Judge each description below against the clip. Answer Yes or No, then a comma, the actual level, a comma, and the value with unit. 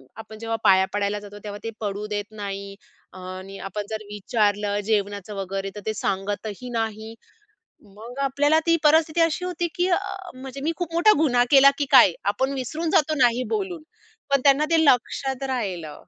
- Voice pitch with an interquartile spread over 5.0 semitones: Yes, wide, 5.6 semitones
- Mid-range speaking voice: No, high, 225 Hz